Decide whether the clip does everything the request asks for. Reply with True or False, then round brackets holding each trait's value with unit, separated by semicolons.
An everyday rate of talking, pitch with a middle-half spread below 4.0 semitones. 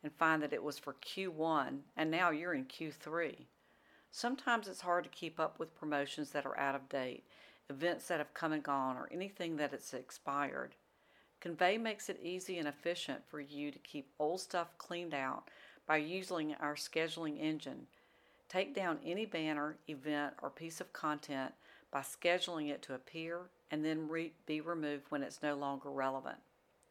True (175 wpm; 3.1 semitones)